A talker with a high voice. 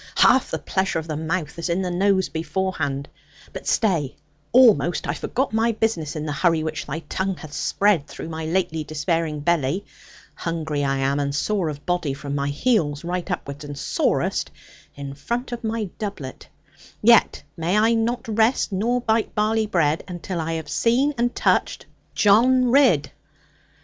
No: medium, 175 Hz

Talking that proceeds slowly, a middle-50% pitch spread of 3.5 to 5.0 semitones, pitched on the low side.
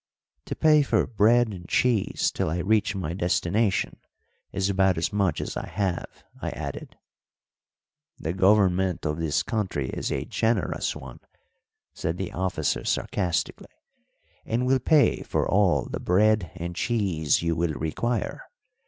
No: average, 145 wpm; average, 4.1 semitones; very low, 95 Hz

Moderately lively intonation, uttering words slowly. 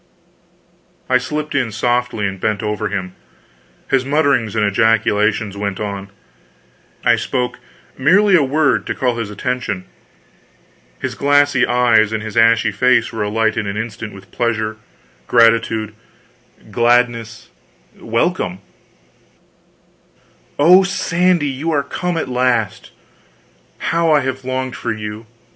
Yes: average, 3.7 semitones; slow, 125 wpm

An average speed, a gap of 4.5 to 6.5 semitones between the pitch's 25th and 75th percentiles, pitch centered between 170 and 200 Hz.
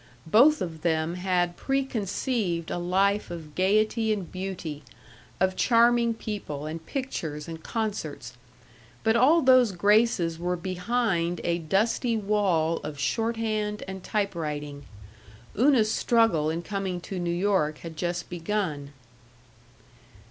No: slow, 120 wpm; average, 4.8 semitones; high, 190 Hz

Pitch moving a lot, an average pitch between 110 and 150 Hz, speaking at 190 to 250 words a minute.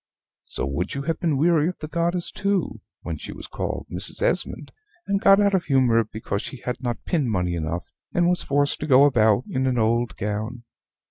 Yes: wide, 7.3 semitones; low, 135 Hz; fast, 205 wpm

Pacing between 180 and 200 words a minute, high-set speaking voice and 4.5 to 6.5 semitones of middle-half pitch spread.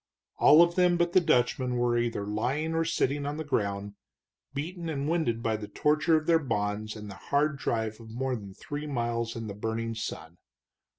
No: average, 195 wpm; low, 125 Hz; wide, 5.5 semitones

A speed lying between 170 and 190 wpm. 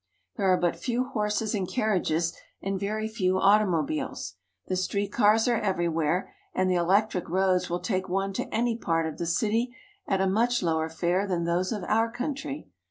Yes: average, 180 wpm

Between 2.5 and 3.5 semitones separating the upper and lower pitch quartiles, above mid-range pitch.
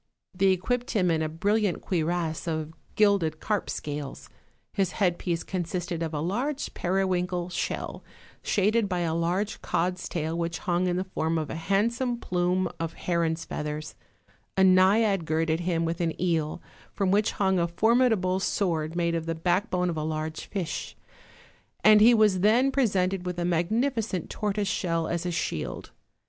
No: average, 3.2 semitones; medium, 180 Hz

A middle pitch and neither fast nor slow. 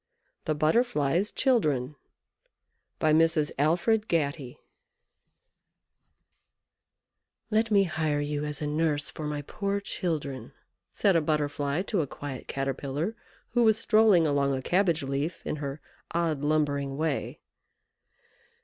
No: medium, 155 Hz; slow, 120 wpm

